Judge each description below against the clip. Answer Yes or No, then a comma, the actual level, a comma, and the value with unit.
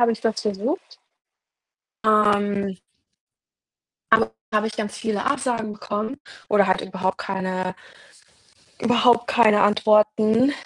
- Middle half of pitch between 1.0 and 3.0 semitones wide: Yes, narrow, 2.4 semitones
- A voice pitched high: Yes, high, 215 Hz